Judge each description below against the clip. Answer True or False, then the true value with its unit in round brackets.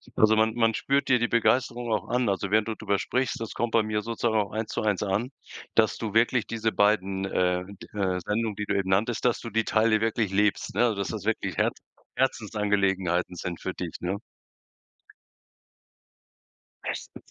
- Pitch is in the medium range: False (110 Hz)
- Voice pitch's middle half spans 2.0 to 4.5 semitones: True (2.5 semitones)